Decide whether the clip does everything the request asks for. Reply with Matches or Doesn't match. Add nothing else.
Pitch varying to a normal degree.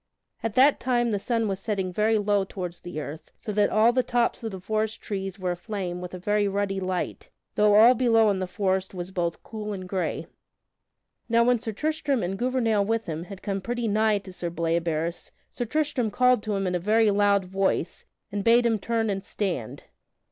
Matches